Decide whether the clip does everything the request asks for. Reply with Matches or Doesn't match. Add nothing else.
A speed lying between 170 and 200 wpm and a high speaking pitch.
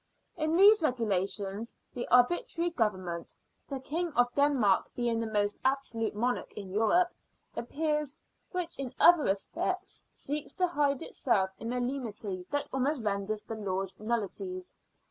Doesn't match